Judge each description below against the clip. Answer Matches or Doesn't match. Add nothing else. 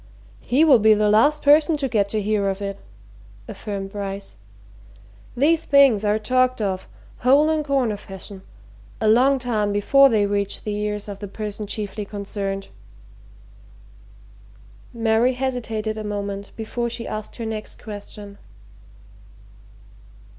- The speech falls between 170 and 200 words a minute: Doesn't match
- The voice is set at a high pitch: Matches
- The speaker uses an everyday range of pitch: Matches